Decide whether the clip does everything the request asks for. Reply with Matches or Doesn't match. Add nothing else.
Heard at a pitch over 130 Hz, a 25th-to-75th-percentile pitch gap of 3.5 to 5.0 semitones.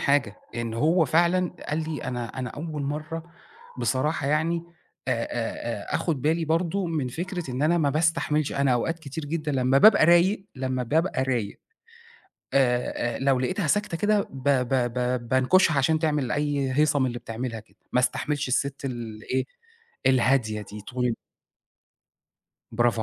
Matches